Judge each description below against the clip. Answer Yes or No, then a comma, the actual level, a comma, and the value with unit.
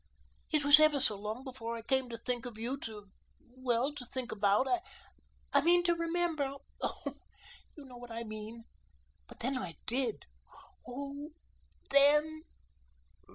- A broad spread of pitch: No, average, 3.9 semitones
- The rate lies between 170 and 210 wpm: No, average, 150 wpm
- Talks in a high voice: Yes, very high, 255 Hz